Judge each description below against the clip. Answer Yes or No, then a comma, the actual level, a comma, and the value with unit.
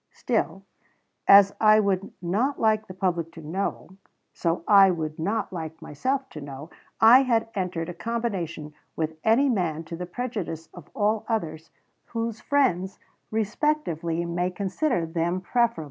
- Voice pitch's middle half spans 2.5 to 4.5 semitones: No, average, 5.2 semitones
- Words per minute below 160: Yes, average, 145 wpm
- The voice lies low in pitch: No, high, 190 Hz